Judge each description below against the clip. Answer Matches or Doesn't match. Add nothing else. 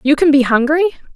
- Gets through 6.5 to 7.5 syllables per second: Matches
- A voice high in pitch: Matches